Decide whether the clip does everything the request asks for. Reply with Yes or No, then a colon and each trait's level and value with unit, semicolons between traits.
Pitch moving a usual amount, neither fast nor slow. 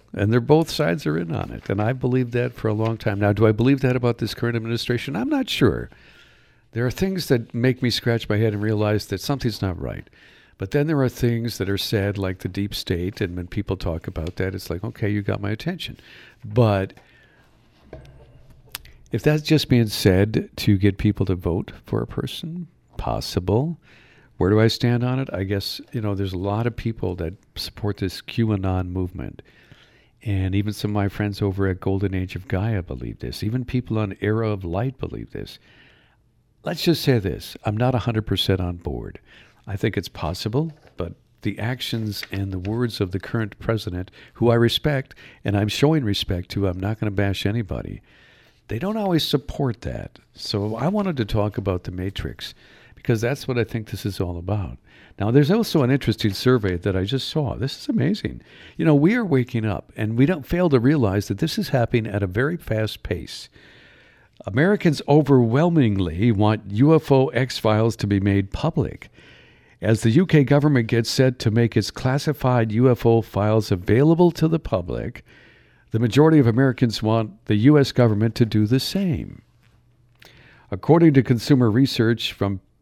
Yes: average, 4.5 semitones; average, 190 wpm